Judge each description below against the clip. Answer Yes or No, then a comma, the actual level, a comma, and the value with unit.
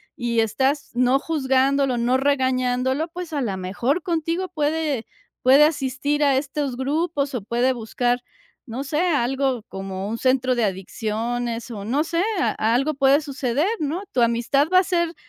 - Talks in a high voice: Yes, very high, 265 Hz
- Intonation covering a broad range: No, average, 3.6 semitones